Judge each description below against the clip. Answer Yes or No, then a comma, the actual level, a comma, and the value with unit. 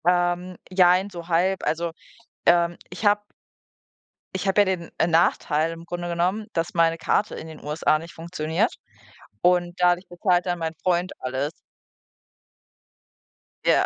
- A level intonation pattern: Yes, narrow, 1.7 semitones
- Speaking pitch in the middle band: Yes, medium, 175 Hz